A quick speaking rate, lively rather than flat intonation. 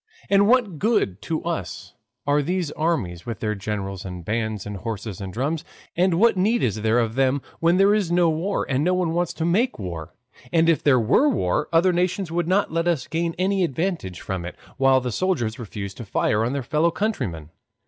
Yes: fast, 210 wpm; wide, 8.5 semitones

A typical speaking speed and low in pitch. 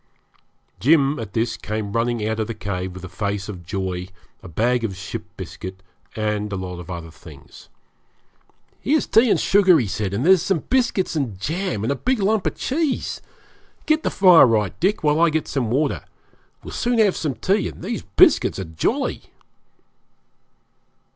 Yes: average, 175 wpm; low, 115 Hz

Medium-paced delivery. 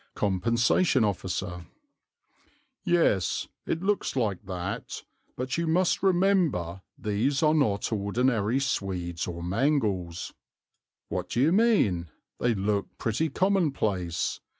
No: slow, 110 wpm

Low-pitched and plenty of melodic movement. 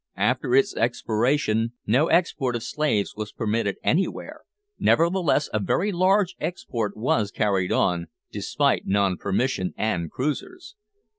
Yes: low, 115 Hz; wide, 7.0 semitones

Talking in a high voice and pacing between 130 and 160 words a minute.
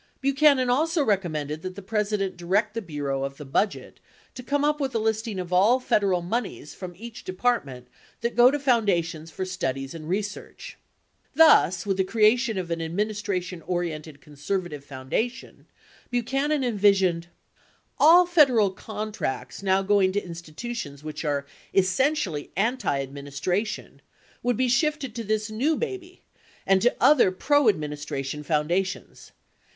Yes: high, 195 Hz; average, 140 wpm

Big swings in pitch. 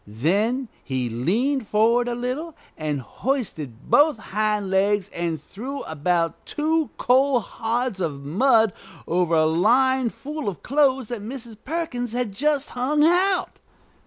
Yes: wide, 7.1 semitones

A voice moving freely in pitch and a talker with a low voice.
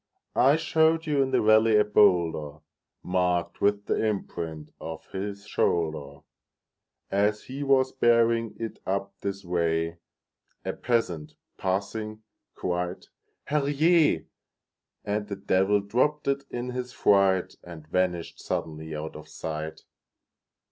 Yes: wide, 5.8 semitones; low, 100 Hz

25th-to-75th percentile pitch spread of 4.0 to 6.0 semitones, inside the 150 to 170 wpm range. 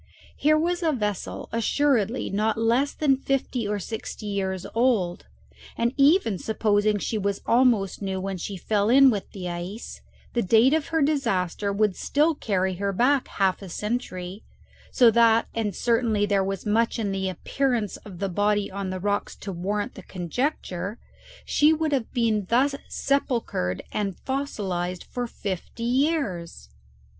Yes: average, 4.5 semitones; average, 155 wpm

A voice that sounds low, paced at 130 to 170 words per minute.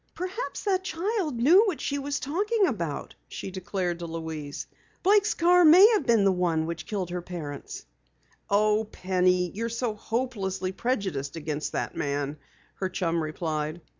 No: high, 195 Hz; average, 155 wpm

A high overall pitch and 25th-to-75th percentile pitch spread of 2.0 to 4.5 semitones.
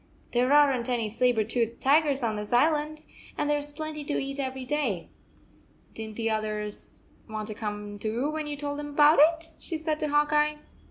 No: very high, 275 Hz; average, 5.0 semitones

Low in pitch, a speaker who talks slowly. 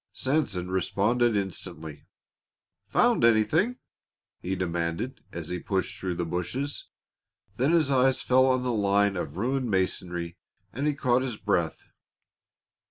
Yes: low, 100 Hz; slow, 130 wpm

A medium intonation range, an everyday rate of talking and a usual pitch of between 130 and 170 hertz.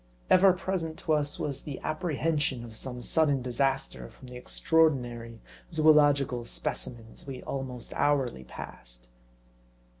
No: average, 4.2 semitones; slow, 120 wpm; low, 135 Hz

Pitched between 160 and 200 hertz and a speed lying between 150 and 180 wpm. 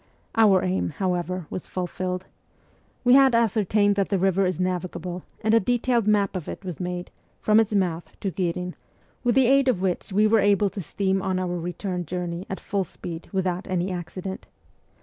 No: high, 190 Hz; average, 195 wpm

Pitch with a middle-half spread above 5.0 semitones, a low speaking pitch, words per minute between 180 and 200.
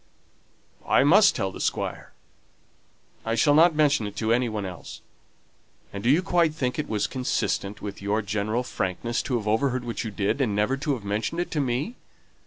Yes: wide, 5.5 semitones; low, 120 Hz; average, 195 wpm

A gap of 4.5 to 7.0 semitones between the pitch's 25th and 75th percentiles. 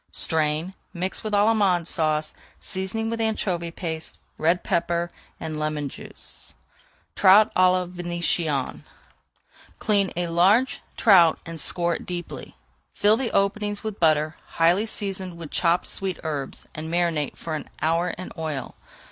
No: average, 3.4 semitones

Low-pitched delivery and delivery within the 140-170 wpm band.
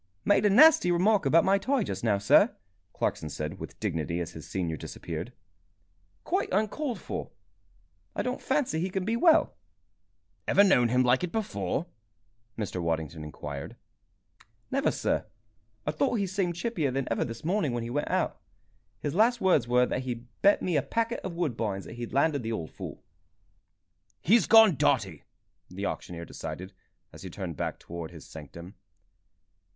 Yes: low, 130 Hz; average, 165 wpm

